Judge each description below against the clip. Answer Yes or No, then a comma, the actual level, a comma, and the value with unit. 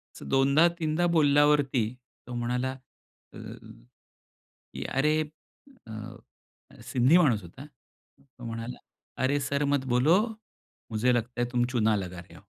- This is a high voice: No, low, 130 Hz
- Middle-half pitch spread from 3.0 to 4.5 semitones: Yes, average, 3.7 semitones